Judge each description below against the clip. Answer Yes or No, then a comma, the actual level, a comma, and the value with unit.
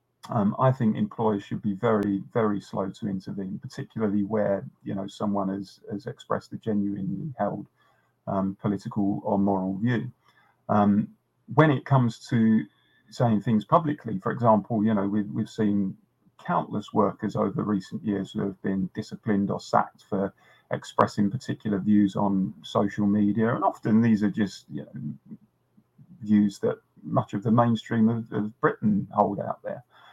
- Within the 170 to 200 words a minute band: No, average, 155 wpm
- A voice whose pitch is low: Yes, low, 105 Hz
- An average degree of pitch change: No, narrow, 2.1 semitones